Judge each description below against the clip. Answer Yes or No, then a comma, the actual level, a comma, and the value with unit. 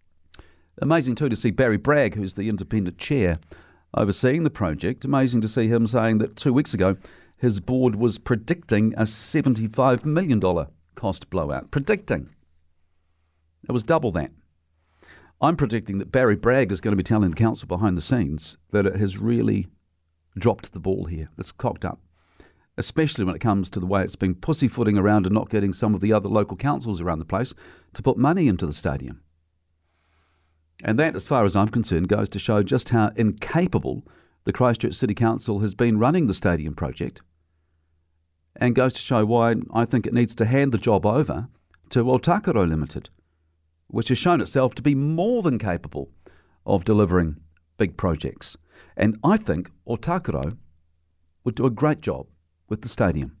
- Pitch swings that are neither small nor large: No, wide, 6.5 semitones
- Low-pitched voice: Yes, low, 105 Hz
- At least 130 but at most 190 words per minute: Yes, average, 175 wpm